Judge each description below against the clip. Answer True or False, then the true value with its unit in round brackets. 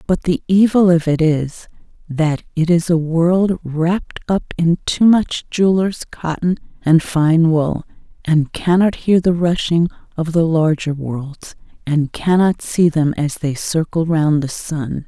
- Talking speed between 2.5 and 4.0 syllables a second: True (3.9 syllables/s)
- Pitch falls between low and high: True (165 Hz)